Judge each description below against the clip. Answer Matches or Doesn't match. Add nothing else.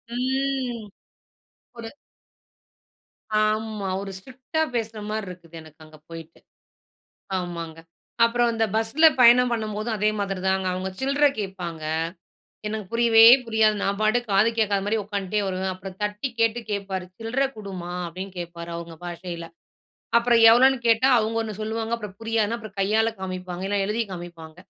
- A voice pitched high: Matches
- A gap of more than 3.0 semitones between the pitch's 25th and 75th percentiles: Matches